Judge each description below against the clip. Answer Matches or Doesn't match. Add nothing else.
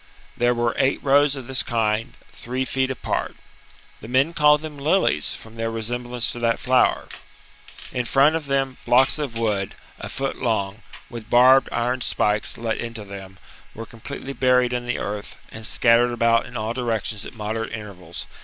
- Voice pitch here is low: Matches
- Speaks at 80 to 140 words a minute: Doesn't match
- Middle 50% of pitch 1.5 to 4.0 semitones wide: Matches